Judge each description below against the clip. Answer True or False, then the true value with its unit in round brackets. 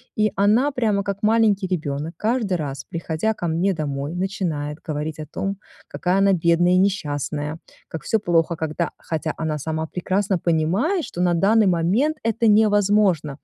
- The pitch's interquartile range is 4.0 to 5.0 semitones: True (4.5 semitones)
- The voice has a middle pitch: True (180 Hz)